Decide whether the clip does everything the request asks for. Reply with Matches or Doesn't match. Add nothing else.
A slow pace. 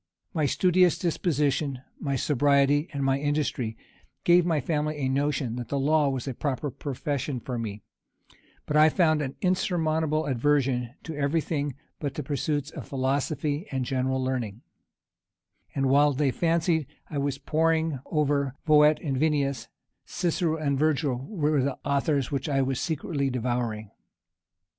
Doesn't match